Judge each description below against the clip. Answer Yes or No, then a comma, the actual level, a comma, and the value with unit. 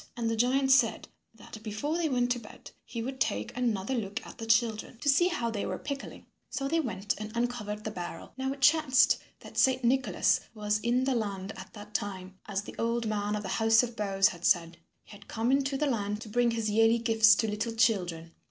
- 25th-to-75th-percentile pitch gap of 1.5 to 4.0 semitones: Yes, average, 3.3 semitones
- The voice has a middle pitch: No, high, 225 Hz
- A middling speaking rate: No, fast, 225 wpm